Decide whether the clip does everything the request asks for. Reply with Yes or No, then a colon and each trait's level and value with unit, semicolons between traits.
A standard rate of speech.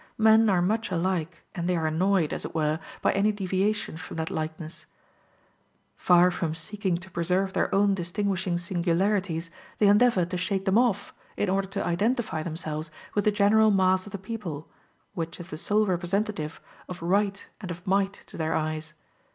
Yes: average, 175 wpm